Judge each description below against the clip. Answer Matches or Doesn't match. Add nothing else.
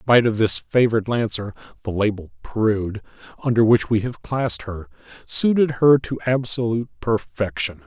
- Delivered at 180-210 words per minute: Doesn't match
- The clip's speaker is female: Doesn't match